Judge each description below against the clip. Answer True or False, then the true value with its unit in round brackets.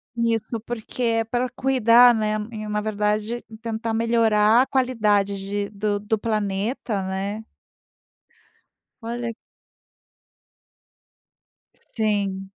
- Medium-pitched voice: False (220 Hz)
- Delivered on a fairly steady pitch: True (2.1 semitones)